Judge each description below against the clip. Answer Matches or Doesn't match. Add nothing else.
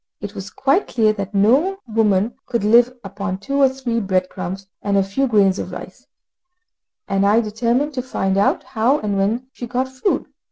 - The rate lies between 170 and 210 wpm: Matches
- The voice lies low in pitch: Doesn't match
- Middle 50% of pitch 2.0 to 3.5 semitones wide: Doesn't match